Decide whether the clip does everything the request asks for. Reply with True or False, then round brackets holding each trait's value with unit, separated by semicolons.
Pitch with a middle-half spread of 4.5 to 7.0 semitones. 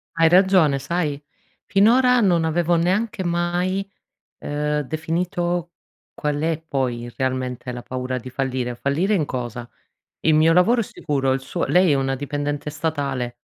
True (4.8 semitones)